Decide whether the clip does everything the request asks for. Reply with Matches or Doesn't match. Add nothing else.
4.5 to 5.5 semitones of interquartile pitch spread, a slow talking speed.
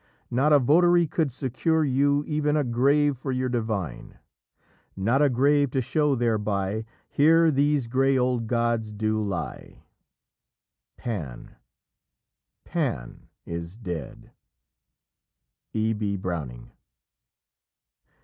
Matches